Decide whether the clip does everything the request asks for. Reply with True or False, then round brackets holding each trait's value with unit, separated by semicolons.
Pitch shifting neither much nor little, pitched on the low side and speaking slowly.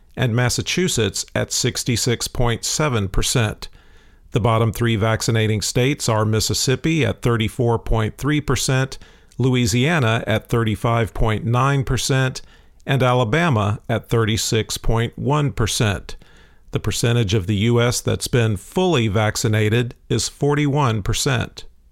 True (3.2 semitones; 115 Hz; 85 wpm)